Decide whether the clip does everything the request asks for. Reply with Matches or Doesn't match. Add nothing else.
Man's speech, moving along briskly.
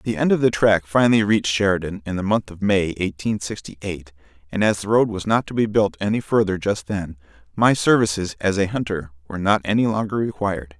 Matches